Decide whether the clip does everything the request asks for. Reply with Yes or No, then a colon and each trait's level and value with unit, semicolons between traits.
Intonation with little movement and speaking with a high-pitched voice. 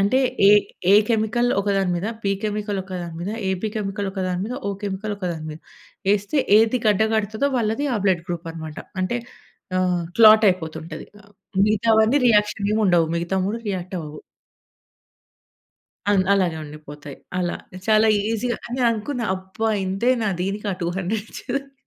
No: average, 3.5 semitones; high, 200 Hz